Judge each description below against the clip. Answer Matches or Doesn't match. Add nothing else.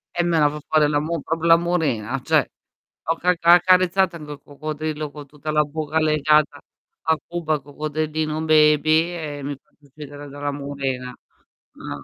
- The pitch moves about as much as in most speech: Doesn't match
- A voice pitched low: Doesn't match